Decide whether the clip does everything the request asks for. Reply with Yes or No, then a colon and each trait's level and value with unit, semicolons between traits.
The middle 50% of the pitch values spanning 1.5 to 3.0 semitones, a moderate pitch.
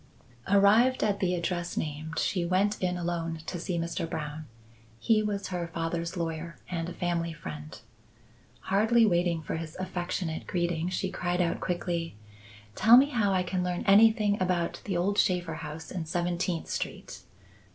Yes: narrow, 2.5 semitones; medium, 175 Hz